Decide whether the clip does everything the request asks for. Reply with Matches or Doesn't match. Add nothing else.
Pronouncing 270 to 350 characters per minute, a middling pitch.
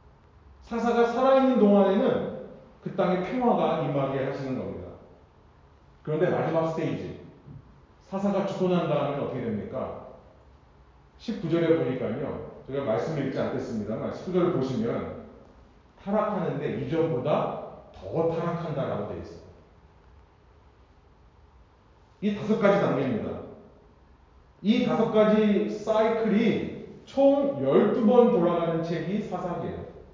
Doesn't match